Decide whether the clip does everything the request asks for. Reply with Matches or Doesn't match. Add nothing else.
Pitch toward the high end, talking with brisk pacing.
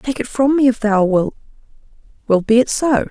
Doesn't match